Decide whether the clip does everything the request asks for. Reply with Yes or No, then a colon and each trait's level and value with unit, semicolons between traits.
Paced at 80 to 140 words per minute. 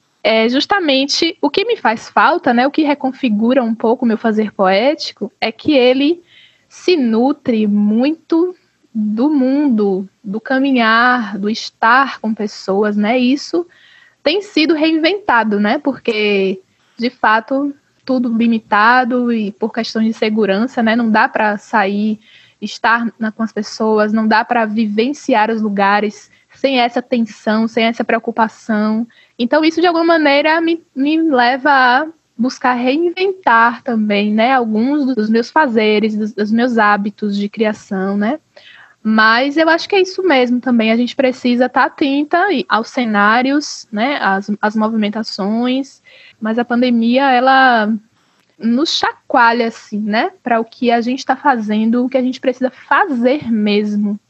No: average, 150 wpm